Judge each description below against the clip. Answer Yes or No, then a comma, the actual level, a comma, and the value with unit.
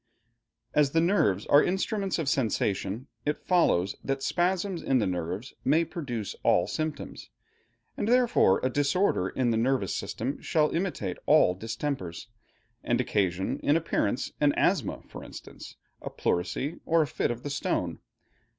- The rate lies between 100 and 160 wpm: Yes, average, 150 wpm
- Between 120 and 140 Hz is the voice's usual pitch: Yes, low, 135 Hz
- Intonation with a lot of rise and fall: Yes, wide, 8.2 semitones